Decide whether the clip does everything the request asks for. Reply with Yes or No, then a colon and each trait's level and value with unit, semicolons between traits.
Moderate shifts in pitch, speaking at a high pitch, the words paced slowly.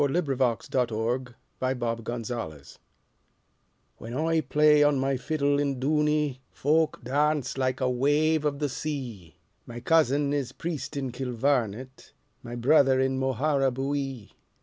No: average, 3.0 semitones; low, 135 Hz; slow, 110 wpm